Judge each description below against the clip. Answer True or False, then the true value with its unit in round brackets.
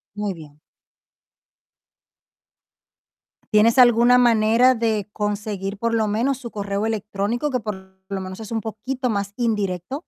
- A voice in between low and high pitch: False (215 Hz)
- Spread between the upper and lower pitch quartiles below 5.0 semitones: True (2.8 semitones)